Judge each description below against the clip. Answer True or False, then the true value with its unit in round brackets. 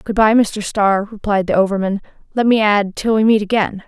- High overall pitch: True (205 Hz)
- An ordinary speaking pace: False (215 wpm)